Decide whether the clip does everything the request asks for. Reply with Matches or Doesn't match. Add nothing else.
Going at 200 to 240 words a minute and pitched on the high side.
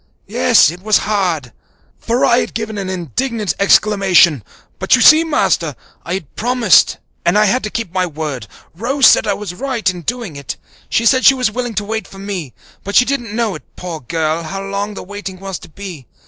Matches